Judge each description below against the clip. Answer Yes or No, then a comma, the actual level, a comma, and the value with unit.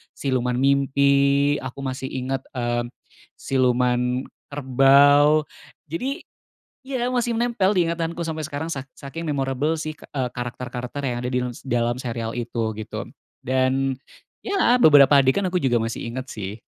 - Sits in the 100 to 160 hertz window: Yes, low, 135 Hz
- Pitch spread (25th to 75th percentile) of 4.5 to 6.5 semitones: No, average, 3.7 semitones